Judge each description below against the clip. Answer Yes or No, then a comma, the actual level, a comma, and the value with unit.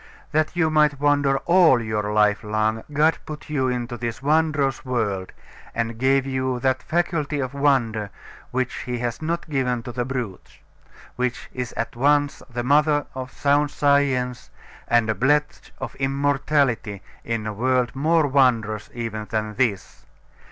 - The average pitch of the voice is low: Yes, low, 130 Hz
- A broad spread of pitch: No, average, 3.8 semitones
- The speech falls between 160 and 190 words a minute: No, average, 150 wpm